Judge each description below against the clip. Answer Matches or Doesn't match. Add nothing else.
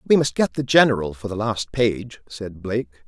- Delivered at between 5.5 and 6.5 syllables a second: Doesn't match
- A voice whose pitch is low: Matches